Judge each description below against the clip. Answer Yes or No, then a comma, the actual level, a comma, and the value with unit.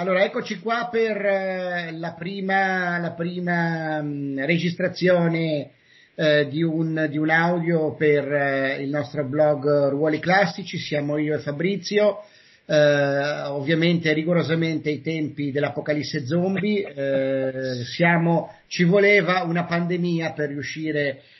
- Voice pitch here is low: No, medium, 160 Hz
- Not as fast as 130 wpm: Yes, average, 120 wpm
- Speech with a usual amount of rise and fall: Yes, average, 3.2 semitones